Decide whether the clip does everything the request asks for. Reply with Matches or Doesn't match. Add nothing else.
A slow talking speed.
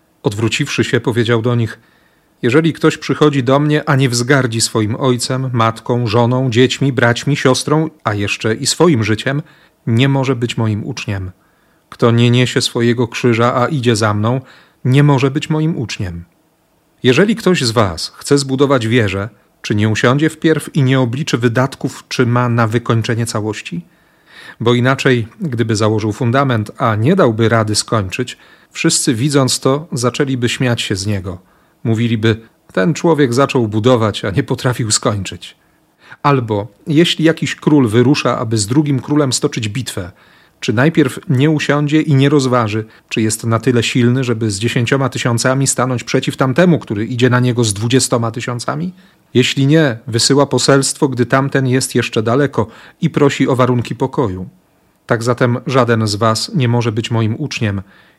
Doesn't match